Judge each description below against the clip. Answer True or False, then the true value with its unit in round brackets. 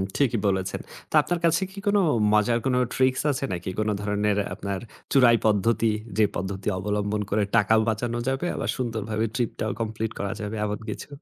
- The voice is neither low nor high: False (110 Hz)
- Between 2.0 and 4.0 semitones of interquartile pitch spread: True (2.8 semitones)